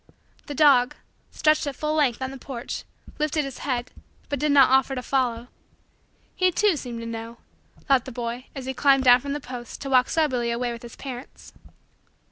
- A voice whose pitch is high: Yes, very high, 260 Hz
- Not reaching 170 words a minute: No, average, 195 wpm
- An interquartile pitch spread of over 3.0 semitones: No, average, 2.7 semitones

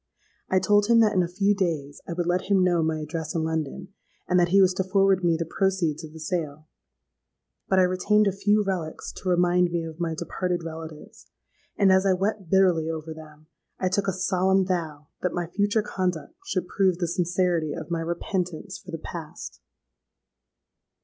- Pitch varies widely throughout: No, average, 2.8 semitones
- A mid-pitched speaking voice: Yes, medium, 180 Hz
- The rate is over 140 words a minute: Yes, average, 195 wpm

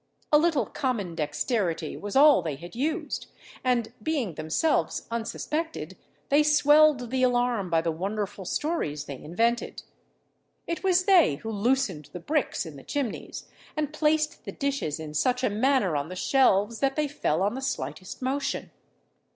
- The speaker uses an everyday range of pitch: No, wide, 8.3 semitones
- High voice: Yes, high, 245 Hz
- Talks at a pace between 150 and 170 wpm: Yes, average, 160 wpm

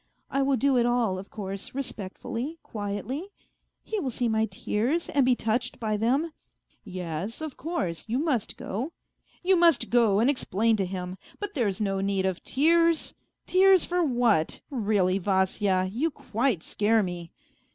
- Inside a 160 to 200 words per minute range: Yes, average, 165 wpm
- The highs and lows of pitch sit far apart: Yes, wide, 6.1 semitones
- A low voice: No, high, 230 Hz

